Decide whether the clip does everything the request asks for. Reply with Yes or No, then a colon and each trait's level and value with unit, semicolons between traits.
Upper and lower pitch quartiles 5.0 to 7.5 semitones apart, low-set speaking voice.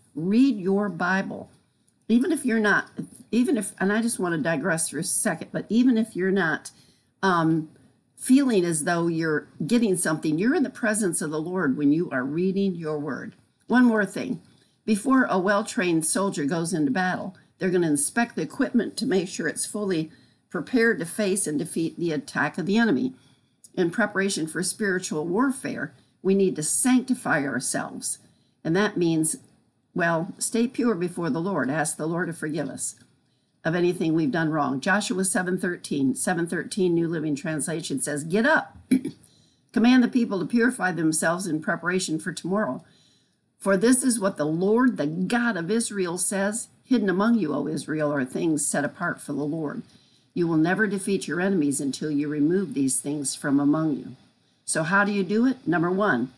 No: wide, 5.5 semitones; medium, 185 Hz